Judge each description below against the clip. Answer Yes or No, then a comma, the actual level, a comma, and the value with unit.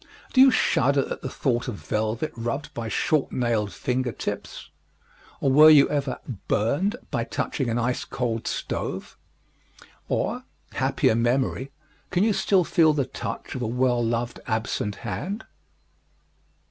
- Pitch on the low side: Yes, low, 125 Hz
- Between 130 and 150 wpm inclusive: Yes, average, 145 wpm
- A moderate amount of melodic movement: Yes, average, 4.2 semitones